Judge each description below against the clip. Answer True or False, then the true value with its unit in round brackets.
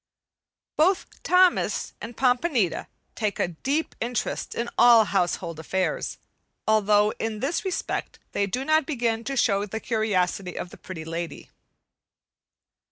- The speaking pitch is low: False (220 Hz)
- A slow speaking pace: True (130 wpm)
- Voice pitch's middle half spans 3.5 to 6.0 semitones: True (5.5 semitones)